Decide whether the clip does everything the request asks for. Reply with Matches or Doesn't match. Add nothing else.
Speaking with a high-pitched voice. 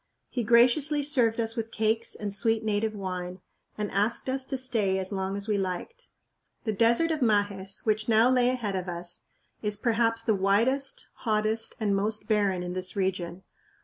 Matches